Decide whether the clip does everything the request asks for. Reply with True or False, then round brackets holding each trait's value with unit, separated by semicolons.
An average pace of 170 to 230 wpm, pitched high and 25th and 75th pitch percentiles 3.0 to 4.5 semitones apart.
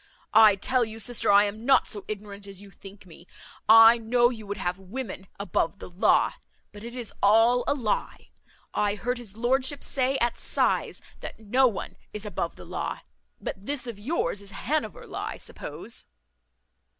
True (180 wpm; 220 Hz; 3.3 semitones)